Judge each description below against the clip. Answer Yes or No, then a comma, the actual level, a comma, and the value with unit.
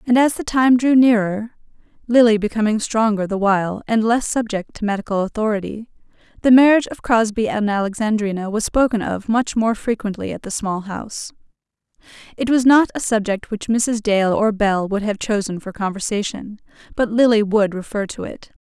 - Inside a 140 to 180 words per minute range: Yes, average, 165 wpm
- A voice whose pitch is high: Yes, high, 220 Hz